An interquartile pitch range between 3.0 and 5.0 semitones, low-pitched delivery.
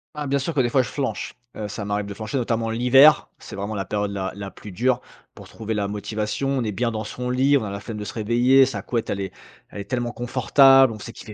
Yes: average, 3.9 semitones; low, 115 Hz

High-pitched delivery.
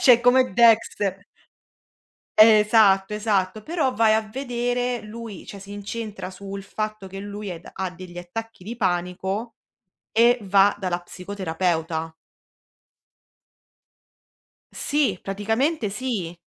Yes: high, 205 Hz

